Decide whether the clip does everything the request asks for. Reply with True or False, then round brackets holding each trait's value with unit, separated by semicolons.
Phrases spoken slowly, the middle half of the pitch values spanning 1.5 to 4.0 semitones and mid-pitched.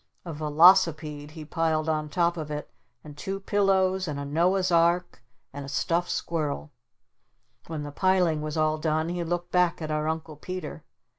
False (170 wpm; 2.6 semitones; 160 Hz)